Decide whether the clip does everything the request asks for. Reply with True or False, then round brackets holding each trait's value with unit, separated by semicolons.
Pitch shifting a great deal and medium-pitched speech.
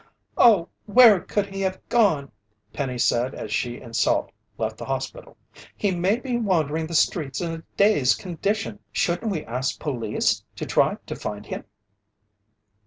True (7.9 semitones; 165 Hz)